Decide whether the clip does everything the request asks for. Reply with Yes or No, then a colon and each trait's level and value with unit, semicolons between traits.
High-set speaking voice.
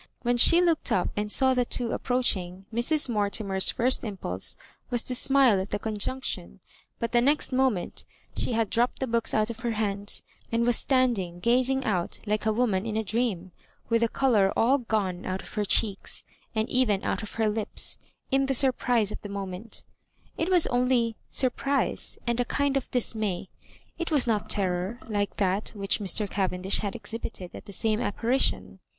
Yes: high, 225 Hz